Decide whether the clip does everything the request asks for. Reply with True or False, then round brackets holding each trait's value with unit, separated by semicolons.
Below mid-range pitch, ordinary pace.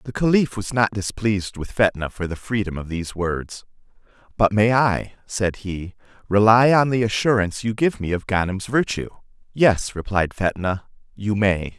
True (105 Hz; 170 wpm)